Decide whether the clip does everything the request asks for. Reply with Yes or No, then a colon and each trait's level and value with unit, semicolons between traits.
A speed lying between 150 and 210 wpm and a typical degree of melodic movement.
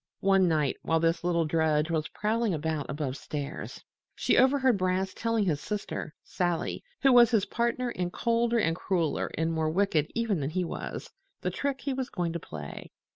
No: average, 180 wpm; wide, 6.3 semitones